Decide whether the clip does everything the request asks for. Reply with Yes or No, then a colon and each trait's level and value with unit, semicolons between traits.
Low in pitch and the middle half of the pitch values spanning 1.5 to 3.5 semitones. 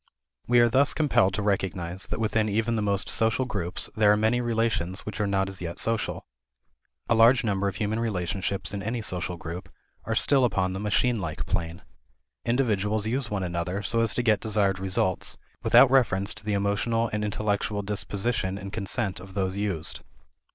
Yes: low, 105 Hz; average, 3.0 semitones